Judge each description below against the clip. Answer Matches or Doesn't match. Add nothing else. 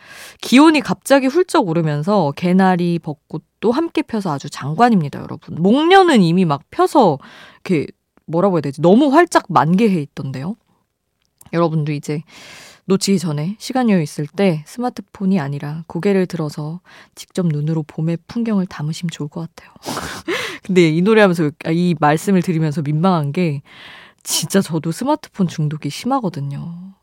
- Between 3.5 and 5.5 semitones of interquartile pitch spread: Matches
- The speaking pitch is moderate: Matches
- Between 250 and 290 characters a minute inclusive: Doesn't match